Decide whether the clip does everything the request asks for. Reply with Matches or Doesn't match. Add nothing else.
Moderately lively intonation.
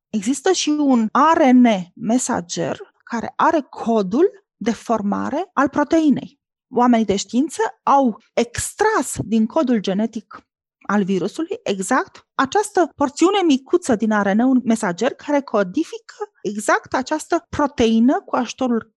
Doesn't match